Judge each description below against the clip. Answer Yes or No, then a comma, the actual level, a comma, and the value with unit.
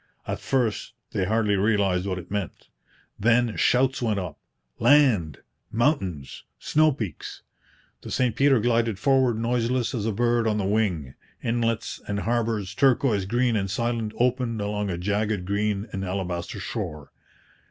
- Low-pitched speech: Yes, low, 110 Hz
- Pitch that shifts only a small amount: No, average, 3.5 semitones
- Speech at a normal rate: Yes, average, 145 wpm